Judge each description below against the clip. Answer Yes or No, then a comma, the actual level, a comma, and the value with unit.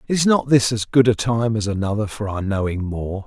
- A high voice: No, low, 110 Hz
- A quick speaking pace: Yes, fast, 240 wpm